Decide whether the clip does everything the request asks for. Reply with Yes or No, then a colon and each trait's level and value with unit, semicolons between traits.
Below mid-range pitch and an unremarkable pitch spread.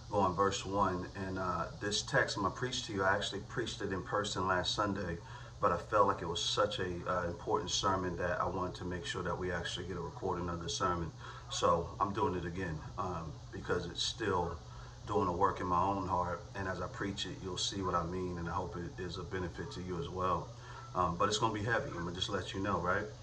No: very low, 95 Hz; narrow, 2.1 semitones